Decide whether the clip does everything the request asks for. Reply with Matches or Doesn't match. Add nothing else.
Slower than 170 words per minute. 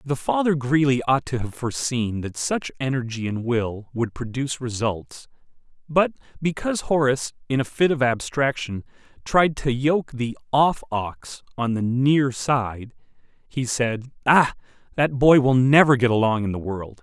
Matches